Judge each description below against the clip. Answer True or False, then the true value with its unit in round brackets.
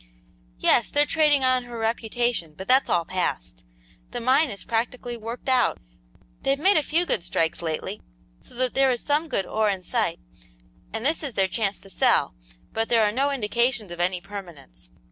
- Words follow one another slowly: False (185 wpm)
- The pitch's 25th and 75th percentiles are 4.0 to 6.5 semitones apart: True (5.4 semitones)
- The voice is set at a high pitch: True (230 Hz)